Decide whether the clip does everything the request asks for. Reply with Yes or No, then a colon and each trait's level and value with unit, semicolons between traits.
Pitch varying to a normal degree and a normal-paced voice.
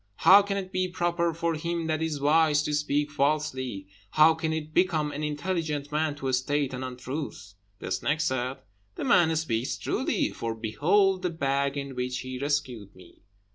Yes: average, 3.7 semitones; average, 175 wpm